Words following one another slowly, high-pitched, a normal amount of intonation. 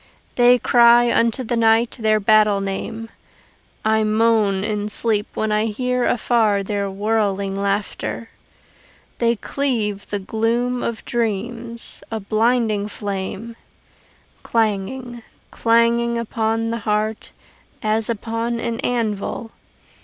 No: slow, 110 wpm; high, 225 Hz; narrow, 2.0 semitones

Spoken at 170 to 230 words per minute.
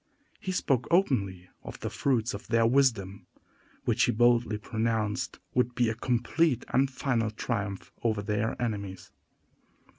No: average, 140 wpm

